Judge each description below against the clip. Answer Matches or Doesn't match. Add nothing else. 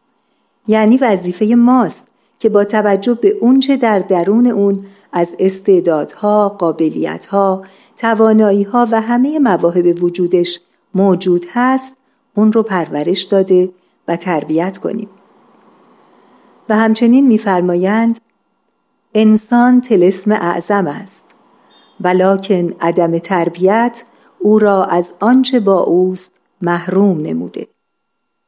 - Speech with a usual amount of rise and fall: Matches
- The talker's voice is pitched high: Matches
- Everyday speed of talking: Doesn't match